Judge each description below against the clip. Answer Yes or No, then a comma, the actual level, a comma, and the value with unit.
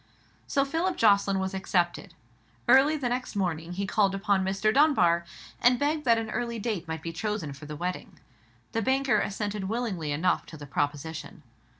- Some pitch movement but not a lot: No, wide, 5.8 semitones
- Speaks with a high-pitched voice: Yes, high, 200 Hz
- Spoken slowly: No, average, 180 wpm